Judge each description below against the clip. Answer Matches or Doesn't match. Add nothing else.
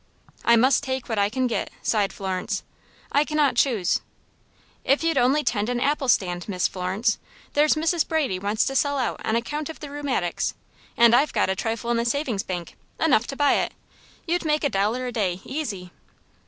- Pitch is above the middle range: Matches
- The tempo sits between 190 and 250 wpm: Matches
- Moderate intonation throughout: Doesn't match